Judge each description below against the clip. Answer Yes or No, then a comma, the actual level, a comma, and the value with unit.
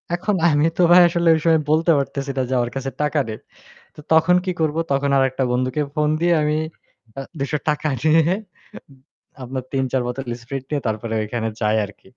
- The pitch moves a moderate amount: Yes, average, 3.6 semitones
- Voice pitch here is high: No, medium, 140 Hz